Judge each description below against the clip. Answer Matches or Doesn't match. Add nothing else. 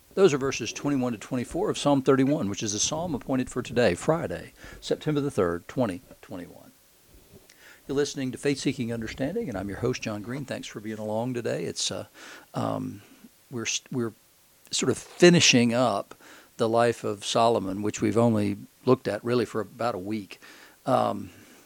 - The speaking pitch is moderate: Doesn't match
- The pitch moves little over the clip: Doesn't match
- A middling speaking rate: Matches